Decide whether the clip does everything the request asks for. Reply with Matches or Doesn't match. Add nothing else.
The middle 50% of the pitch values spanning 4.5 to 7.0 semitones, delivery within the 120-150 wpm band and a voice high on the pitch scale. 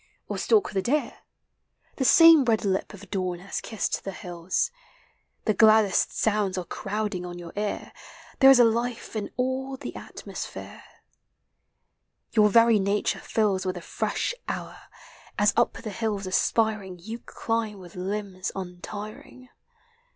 Doesn't match